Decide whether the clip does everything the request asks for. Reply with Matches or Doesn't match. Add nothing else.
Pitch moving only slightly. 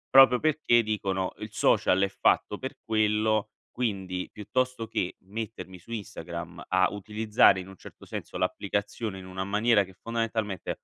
Doesn't match